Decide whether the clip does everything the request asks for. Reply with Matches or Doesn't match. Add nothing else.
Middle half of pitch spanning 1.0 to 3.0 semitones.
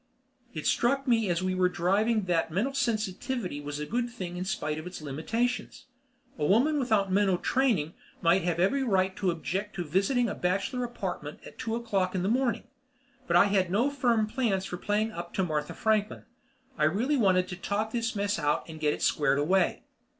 Doesn't match